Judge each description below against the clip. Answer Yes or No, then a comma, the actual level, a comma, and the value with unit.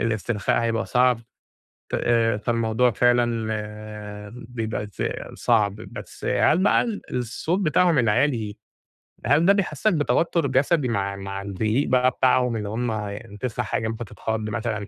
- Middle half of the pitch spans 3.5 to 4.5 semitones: No, average, 3.0 semitones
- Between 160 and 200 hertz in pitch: No, low, 115 Hz